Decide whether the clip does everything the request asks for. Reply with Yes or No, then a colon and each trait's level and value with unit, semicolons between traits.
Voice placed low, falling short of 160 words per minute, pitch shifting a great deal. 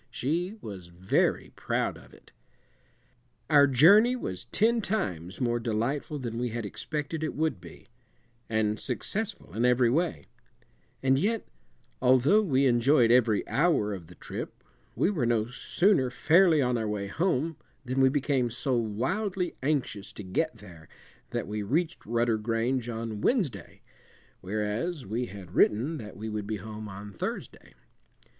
Yes: low, 120 Hz; average, 150 wpm; wide, 6.3 semitones